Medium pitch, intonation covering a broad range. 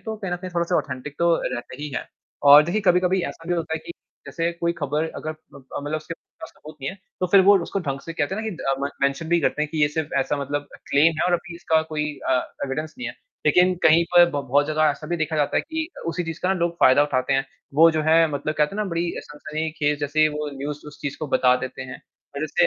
No: medium, 155 Hz; average, 2.9 semitones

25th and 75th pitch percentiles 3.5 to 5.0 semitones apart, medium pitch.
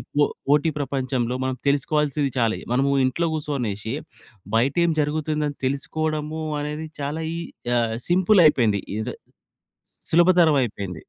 Yes: average, 3.8 semitones; medium, 145 Hz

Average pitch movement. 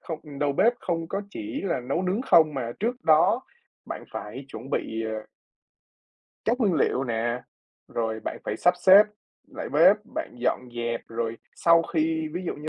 No: wide, 7.1 semitones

